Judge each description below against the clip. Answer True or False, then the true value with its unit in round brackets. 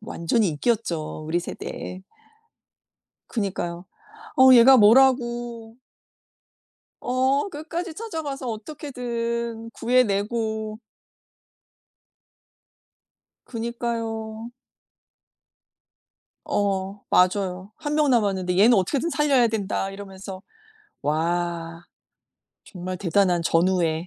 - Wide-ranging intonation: False (4.8 semitones)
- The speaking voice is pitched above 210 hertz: True (220 Hz)